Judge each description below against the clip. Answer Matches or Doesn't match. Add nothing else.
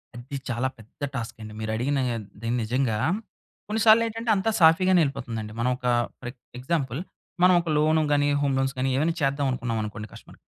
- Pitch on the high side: Doesn't match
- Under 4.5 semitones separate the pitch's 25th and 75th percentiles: Doesn't match